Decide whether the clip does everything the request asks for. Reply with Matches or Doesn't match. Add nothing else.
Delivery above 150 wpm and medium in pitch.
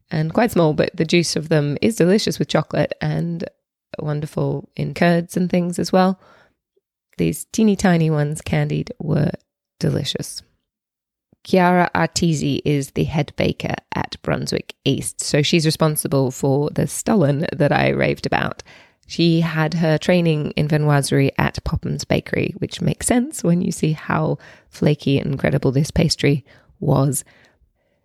Doesn't match